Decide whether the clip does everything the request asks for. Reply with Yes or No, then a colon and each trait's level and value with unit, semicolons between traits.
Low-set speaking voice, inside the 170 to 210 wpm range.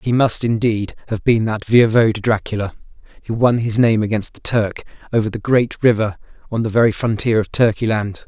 Yes: low, 110 Hz; average, 190 wpm